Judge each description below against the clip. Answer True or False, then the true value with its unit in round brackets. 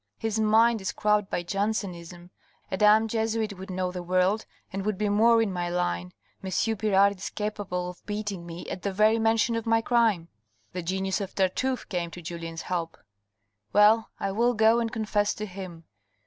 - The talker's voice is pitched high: True (200 Hz)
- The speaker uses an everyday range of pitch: True (3.4 semitones)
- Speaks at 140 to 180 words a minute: False (190 wpm)